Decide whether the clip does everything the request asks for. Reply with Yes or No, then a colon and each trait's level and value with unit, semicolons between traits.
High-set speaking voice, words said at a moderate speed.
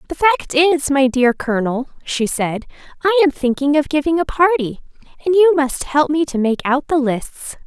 Yes: very high, 285 Hz; average, 195 wpm